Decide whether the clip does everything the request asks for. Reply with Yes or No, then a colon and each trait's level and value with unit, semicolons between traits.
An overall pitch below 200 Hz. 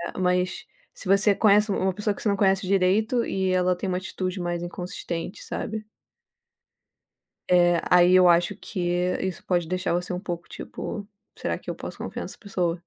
Yes: medium, 185 Hz